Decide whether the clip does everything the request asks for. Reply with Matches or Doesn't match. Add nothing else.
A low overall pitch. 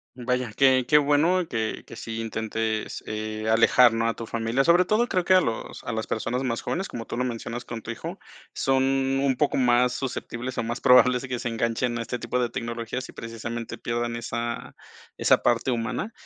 Matches